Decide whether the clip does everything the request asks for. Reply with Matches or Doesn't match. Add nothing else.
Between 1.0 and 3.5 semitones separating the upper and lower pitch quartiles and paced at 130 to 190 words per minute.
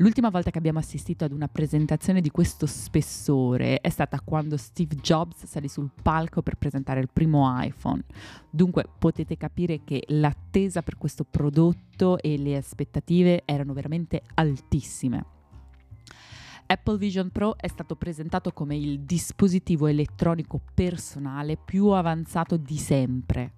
Matches